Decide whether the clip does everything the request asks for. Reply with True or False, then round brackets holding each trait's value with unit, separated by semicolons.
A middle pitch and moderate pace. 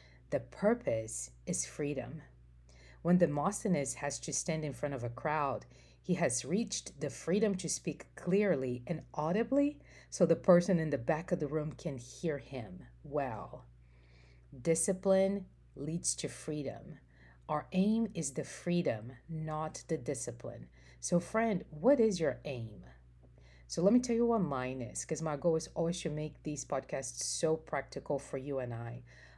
True (150 Hz; 160 wpm)